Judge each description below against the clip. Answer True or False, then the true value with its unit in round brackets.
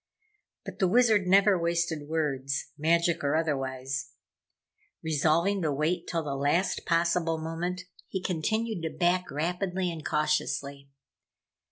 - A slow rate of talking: True (125 wpm)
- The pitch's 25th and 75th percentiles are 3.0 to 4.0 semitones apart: True (3.4 semitones)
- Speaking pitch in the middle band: True (165 Hz)